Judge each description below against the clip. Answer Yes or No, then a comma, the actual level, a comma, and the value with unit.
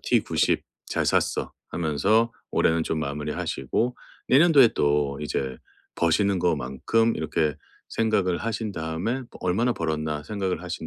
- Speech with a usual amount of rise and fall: No, wide, 6.5 semitones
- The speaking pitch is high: No, very low, 85 Hz